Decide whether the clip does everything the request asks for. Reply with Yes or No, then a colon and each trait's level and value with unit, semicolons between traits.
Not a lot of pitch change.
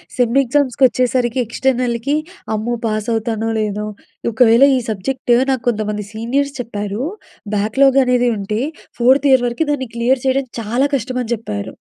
No: average, 3.1 semitones